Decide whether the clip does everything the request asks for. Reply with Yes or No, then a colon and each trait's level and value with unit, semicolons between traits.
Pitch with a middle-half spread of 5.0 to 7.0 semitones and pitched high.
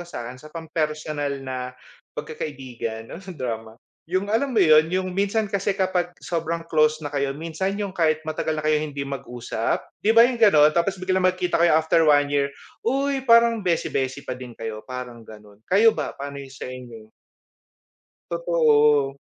No: wide, 5.5 semitones; medium, 155 Hz